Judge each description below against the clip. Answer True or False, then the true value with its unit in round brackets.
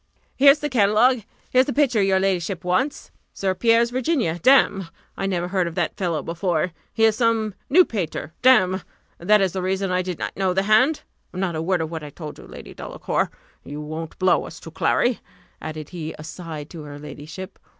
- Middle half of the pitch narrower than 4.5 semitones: False (5.2 semitones)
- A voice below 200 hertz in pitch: True (190 Hz)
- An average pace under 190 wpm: False (195 wpm)